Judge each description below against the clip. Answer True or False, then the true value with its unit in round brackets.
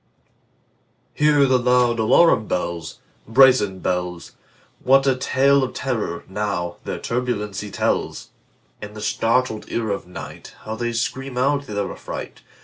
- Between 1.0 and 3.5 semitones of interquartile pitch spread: False (4.2 semitones)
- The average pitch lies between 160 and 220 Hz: False (115 Hz)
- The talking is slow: True (115 wpm)